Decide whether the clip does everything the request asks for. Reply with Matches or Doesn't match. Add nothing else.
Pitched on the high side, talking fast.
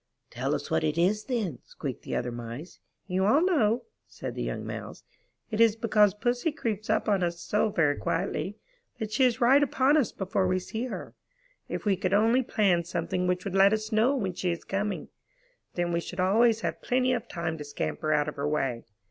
Matches